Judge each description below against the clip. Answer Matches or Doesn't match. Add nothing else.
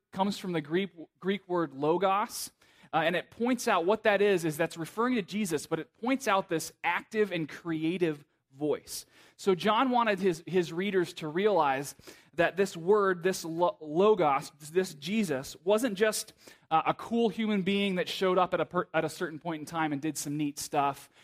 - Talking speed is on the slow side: Doesn't match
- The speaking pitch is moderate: Matches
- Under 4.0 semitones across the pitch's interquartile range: Doesn't match